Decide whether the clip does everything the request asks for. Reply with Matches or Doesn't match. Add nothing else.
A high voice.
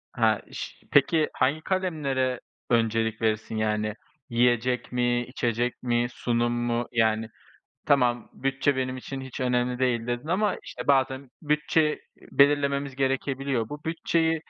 Doesn't match